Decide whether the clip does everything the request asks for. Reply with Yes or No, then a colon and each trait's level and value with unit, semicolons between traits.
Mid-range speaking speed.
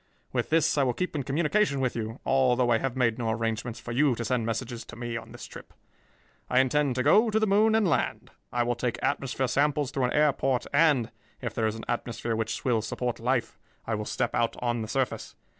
No: fast, 230 wpm